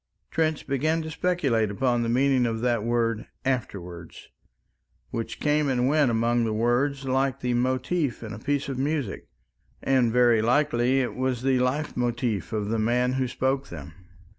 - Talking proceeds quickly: No, average, 165 wpm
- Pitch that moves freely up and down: No, average, 2.8 semitones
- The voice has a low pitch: Yes, low, 125 Hz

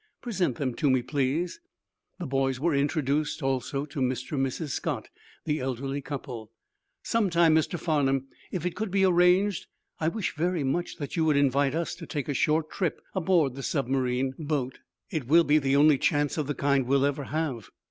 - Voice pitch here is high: No, medium, 145 Hz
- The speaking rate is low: No, average, 190 wpm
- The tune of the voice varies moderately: Yes, average, 3.6 semitones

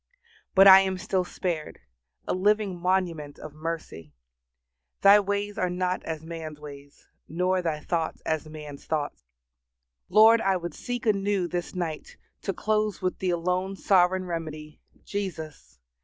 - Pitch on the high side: No, medium, 180 Hz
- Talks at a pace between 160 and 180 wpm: No, average, 140 wpm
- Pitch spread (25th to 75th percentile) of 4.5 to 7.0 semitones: No, average, 3.5 semitones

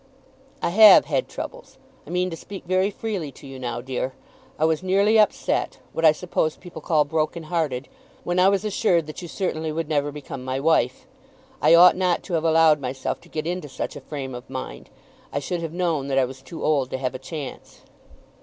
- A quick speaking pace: Yes, fast, 210 wpm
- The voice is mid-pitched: Yes, medium, 160 Hz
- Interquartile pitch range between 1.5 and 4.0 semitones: No, average, 4.6 semitones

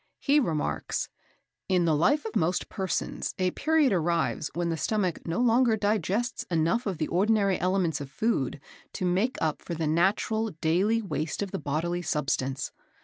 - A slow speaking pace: No, average, 165 wpm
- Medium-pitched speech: Yes, medium, 180 Hz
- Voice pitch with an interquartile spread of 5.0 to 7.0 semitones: Yes, average, 5.3 semitones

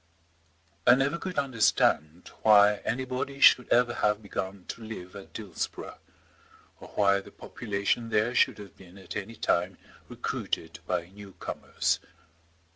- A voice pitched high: No, low, 105 Hz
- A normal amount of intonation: Yes, average, 3.9 semitones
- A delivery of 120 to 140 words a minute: Yes, slow, 135 wpm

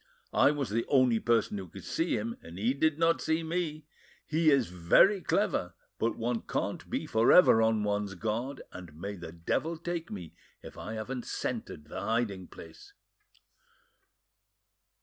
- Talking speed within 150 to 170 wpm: Yes, average, 165 wpm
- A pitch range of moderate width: No, wide, 7.4 semitones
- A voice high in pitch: No, low, 115 Hz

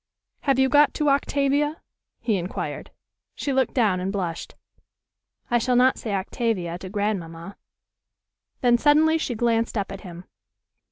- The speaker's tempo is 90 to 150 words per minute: Yes, average, 145 wpm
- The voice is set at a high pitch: Yes, high, 230 Hz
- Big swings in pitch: Yes, wide, 6.1 semitones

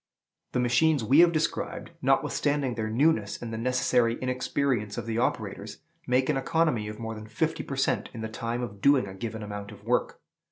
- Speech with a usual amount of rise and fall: Yes, average, 3.4 semitones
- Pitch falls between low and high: No, low, 120 Hz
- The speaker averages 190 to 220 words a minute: Yes, average, 195 wpm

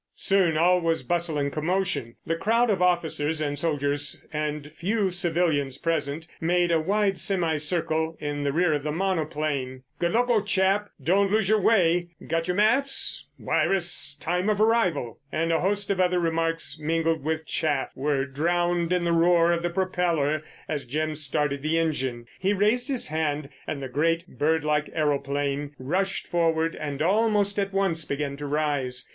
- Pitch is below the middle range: No, medium, 165 Hz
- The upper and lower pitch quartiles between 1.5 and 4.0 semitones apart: Yes, average, 3.6 semitones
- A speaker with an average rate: Yes, average, 170 wpm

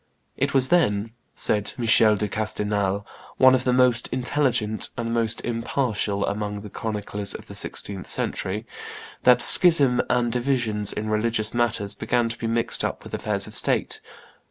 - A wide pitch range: No, average, 2.9 semitones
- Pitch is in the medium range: No, low, 115 Hz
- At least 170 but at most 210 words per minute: No, average, 155 wpm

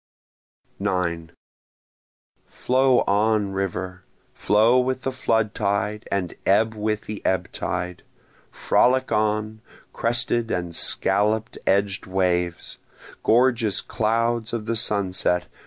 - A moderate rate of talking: No, slow, 105 wpm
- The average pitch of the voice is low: Yes, low, 105 Hz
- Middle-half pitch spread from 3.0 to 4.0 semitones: Yes, average, 3.3 semitones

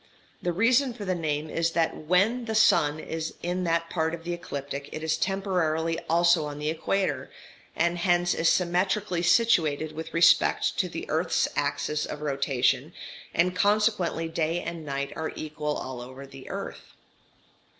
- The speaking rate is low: No, average, 160 wpm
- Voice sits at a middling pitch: Yes, medium, 165 Hz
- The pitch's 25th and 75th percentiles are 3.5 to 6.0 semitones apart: No, average, 3.0 semitones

